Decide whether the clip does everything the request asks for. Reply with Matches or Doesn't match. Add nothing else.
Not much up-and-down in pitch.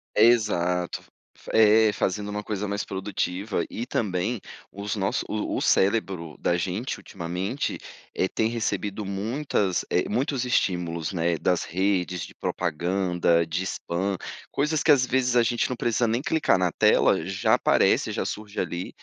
Doesn't match